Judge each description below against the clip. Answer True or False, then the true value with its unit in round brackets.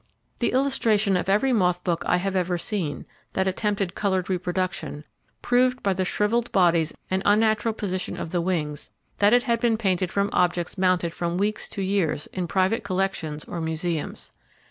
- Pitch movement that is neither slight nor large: True (3.0 semitones)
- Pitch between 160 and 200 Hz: True (190 Hz)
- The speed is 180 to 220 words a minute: False (170 wpm)